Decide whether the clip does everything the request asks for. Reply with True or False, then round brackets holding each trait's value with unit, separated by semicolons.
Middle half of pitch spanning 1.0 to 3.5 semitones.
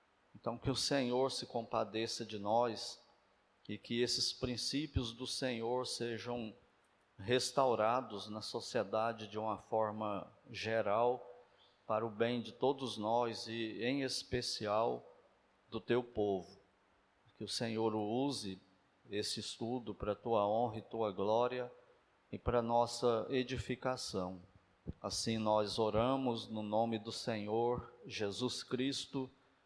True (2.7 semitones)